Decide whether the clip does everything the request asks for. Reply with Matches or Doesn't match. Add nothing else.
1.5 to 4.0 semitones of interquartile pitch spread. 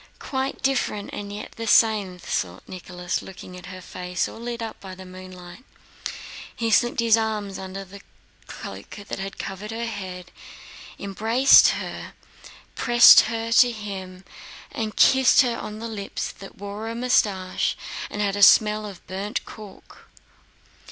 Matches